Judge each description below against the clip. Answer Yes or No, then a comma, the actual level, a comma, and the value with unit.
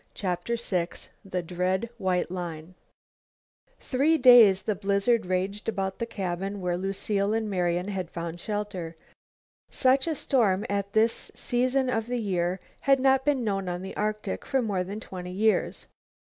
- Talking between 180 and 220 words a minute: No, average, 155 wpm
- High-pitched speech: Yes, high, 200 Hz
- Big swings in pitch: No, average, 4.1 semitones